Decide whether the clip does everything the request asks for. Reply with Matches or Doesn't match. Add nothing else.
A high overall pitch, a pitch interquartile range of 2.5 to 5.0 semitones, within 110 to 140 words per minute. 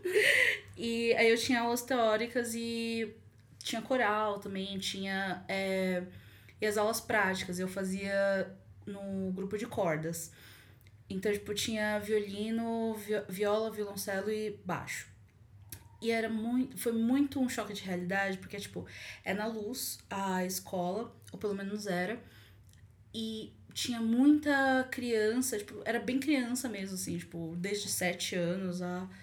Matches